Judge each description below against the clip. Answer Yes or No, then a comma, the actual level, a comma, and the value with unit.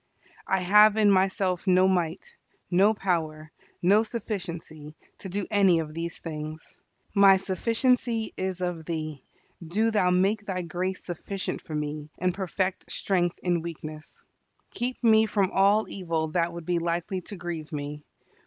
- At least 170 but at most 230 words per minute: No, average, 150 wpm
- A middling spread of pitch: Yes, average, 3.2 semitones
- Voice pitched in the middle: Yes, medium, 180 Hz